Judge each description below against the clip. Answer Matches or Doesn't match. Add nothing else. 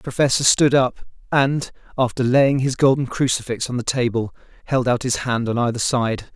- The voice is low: Matches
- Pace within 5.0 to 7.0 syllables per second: Matches